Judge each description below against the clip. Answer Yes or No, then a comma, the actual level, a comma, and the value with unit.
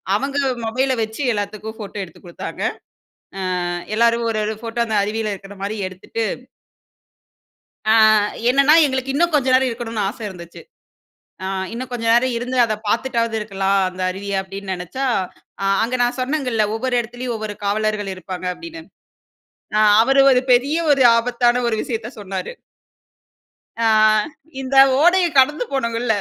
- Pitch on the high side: Yes, high, 230 Hz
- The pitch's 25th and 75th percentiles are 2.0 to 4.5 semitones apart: Yes, average, 3.8 semitones